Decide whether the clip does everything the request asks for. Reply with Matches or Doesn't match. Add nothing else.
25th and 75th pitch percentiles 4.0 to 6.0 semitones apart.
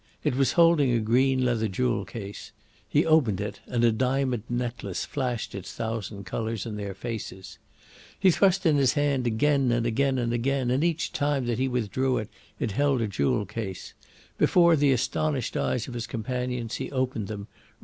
Doesn't match